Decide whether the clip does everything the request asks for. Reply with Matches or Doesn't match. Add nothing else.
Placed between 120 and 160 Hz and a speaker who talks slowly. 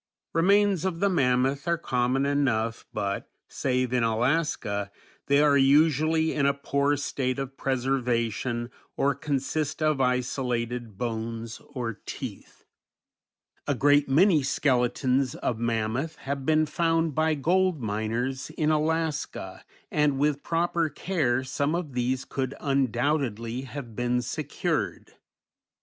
Matches